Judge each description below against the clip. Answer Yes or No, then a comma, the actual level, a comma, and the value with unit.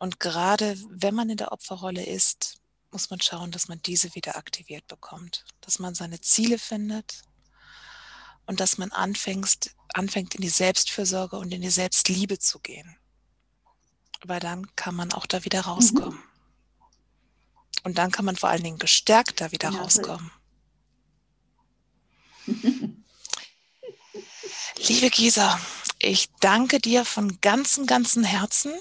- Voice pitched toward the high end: Yes, high, 195 Hz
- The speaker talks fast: No, average, 135 wpm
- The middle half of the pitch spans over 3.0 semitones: Yes, average, 3.8 semitones